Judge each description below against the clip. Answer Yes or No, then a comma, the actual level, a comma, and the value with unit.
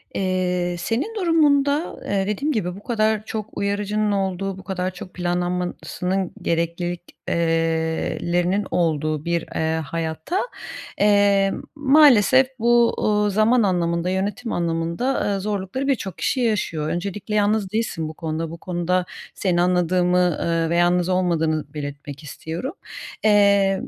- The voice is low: No, medium, 185 Hz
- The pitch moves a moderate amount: Yes, average, 3.6 semitones